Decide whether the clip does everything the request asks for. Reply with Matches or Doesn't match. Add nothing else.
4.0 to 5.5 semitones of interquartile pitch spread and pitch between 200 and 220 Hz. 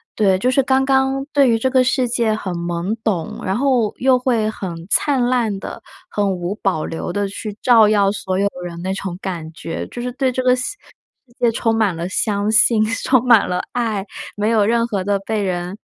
Matches